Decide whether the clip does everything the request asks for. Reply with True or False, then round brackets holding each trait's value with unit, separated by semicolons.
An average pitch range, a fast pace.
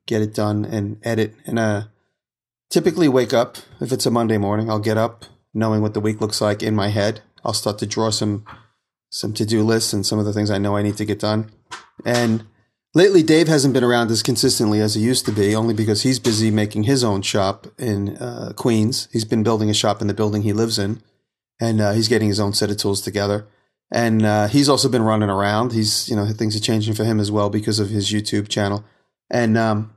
False (1.7 semitones; 230 wpm)